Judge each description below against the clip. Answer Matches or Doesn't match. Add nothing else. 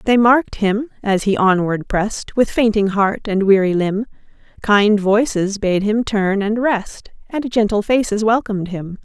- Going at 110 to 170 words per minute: Matches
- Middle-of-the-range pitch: Doesn't match